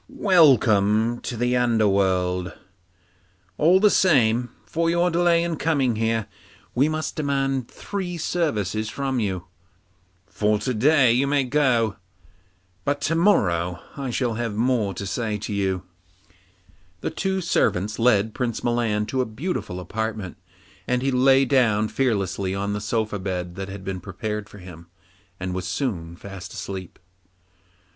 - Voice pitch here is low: Yes, low, 115 Hz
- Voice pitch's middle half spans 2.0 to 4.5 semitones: No, wide, 5.5 semitones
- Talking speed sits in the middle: Yes, average, 145 wpm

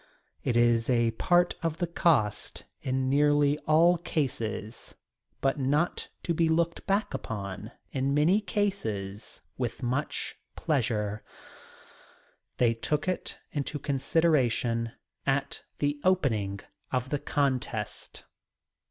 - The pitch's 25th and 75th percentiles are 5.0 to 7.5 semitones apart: Yes, wide, 5.6 semitones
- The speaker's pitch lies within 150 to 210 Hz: No, low, 135 Hz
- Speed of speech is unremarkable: No, slow, 110 wpm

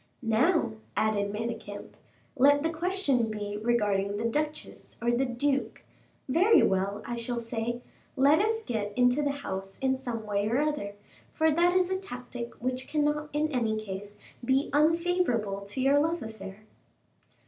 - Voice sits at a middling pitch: No, high, 245 Hz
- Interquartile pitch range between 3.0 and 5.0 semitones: No, wide, 5.6 semitones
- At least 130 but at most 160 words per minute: Yes, average, 155 wpm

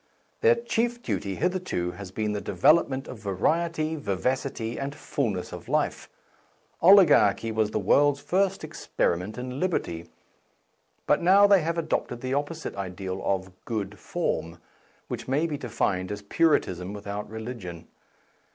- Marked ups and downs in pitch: Yes, wide, 8.5 semitones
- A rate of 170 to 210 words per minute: No, average, 140 wpm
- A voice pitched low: Yes, low, 120 Hz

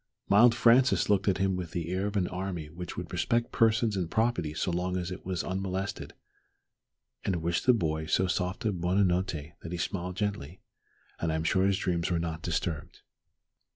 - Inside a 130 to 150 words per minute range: No, average, 200 wpm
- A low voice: Yes, very low, 90 Hz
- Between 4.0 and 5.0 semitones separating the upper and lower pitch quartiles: No, average, 2.7 semitones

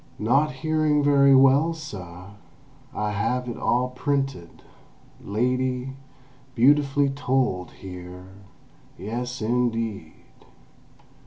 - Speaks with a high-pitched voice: No, low, 125 Hz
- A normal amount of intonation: Yes, average, 4.7 semitones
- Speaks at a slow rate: Yes, slow, 75 wpm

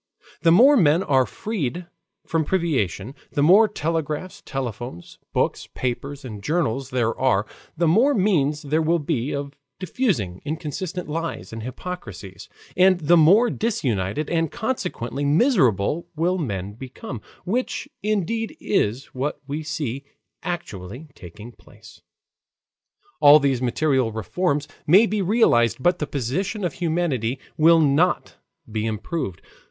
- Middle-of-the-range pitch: Yes, medium, 150 Hz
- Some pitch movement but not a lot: No, wide, 6.2 semitones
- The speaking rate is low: Yes, slow, 130 wpm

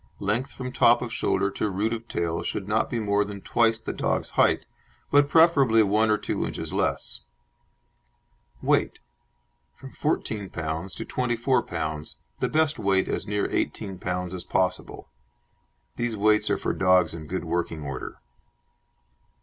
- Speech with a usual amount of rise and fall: Yes, average, 4.4 semitones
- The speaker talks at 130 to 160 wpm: Yes, average, 155 wpm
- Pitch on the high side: No, low, 105 Hz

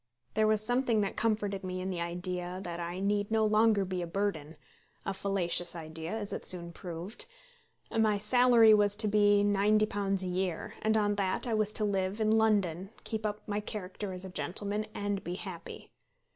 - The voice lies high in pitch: Yes, high, 200 Hz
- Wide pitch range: No, average, 2.7 semitones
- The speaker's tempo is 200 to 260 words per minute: No, average, 185 wpm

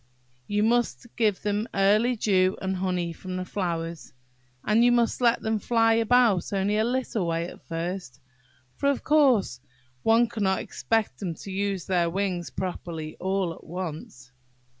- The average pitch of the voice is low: No, high, 195 Hz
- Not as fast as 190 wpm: Yes, average, 160 wpm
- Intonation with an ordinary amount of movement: Yes, average, 4.2 semitones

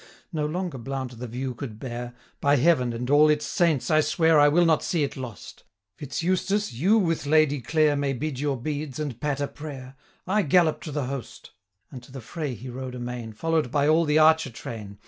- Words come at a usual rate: No, fast, 215 wpm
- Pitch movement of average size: Yes, average, 3.8 semitones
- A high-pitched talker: No, medium, 145 Hz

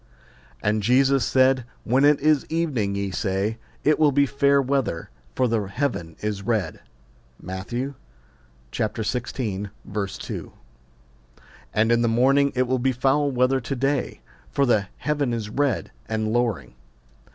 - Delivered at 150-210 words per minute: No, average, 140 wpm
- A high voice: No, low, 125 Hz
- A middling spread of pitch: Yes, average, 4.4 semitones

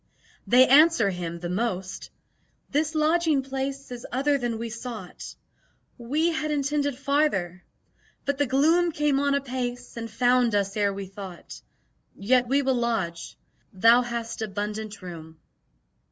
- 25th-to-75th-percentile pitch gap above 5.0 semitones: Yes, wide, 5.5 semitones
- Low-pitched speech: No, high, 245 Hz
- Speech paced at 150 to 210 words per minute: No, average, 140 wpm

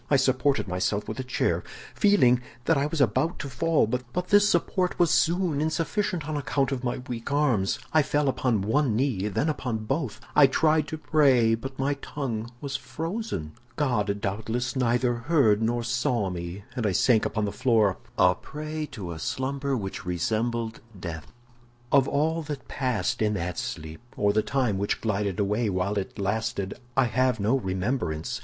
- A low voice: Yes, low, 125 Hz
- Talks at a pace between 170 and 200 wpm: Yes, average, 175 wpm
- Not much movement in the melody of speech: No, wide, 5.6 semitones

